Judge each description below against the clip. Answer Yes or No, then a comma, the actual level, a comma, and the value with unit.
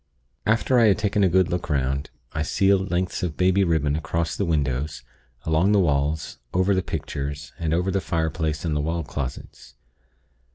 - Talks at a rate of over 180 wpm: No, average, 175 wpm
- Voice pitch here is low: Yes, very low, 80 Hz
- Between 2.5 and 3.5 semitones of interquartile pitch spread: No, average, 3.9 semitones